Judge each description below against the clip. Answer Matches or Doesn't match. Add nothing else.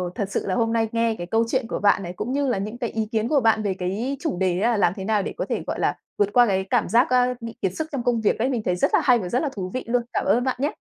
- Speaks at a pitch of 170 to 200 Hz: Doesn't match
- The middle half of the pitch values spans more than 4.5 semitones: Doesn't match